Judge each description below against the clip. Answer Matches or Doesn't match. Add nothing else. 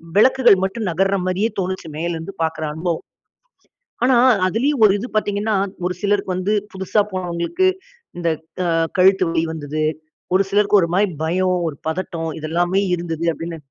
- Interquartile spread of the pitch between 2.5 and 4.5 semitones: Matches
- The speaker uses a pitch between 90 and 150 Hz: Doesn't match